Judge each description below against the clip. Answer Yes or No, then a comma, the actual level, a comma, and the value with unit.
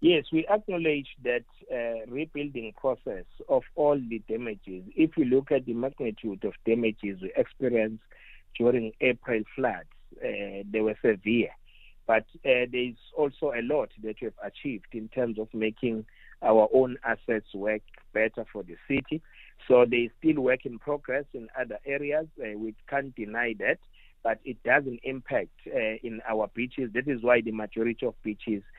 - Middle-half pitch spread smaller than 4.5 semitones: Yes, average, 3.3 semitones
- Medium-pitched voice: No, low, 120 Hz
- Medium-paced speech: Yes, average, 165 wpm